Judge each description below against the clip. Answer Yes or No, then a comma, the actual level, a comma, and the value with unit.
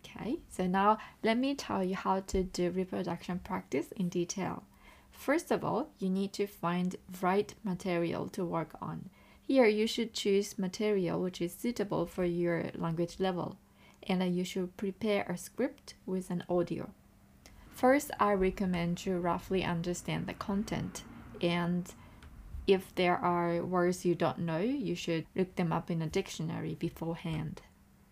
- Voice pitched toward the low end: No, medium, 185 Hz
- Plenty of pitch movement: No, narrow, 2.5 semitones